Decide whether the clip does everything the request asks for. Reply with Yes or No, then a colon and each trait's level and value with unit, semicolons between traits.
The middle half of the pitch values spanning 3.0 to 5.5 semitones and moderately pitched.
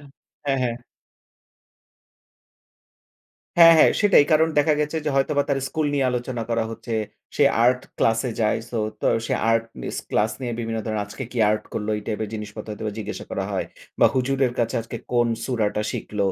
No: average, 3.7 semitones; low, 120 Hz